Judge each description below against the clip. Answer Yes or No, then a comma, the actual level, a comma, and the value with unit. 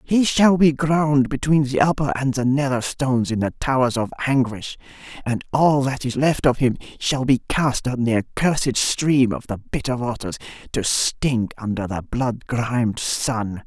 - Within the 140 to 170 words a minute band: No, average, 180 wpm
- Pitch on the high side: No, low, 130 Hz